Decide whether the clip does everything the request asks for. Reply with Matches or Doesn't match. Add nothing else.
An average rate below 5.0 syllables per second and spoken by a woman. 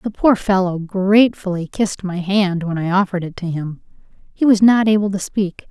Doesn't match